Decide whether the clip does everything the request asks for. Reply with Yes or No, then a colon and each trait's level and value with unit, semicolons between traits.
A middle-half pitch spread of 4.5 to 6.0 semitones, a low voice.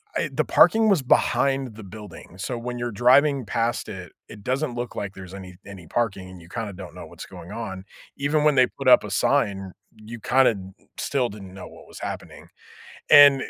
Yes: average, 5.3 semitones; low, 115 Hz